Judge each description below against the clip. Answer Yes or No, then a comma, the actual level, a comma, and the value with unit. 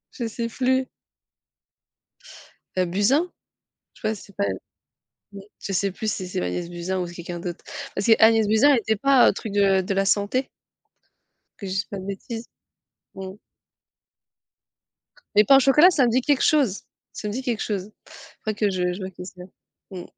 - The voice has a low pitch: No, high, 205 Hz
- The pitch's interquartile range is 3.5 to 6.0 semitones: Yes, average, 4.1 semitones